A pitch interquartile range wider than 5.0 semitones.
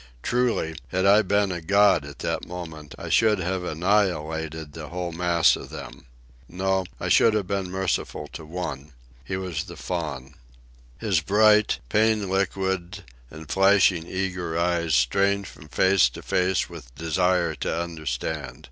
No: average, 3.4 semitones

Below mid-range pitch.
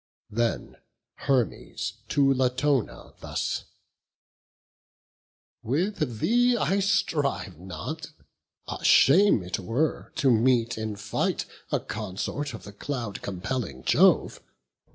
Yes: low, 125 Hz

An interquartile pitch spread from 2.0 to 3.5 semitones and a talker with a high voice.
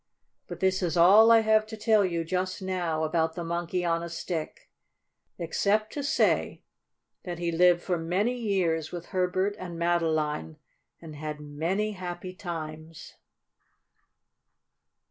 No: average, 2.7 semitones; medium, 175 Hz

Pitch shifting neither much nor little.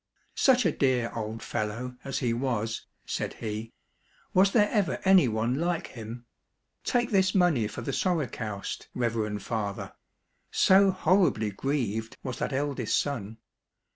No: wide, 8.0 semitones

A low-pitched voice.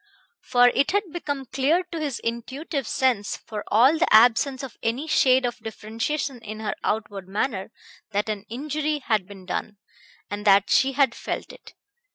No: high, 245 Hz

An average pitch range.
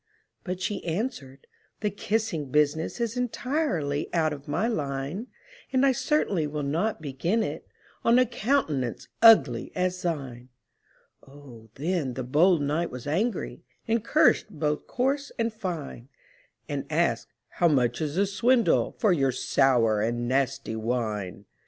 No: wide, 8.2 semitones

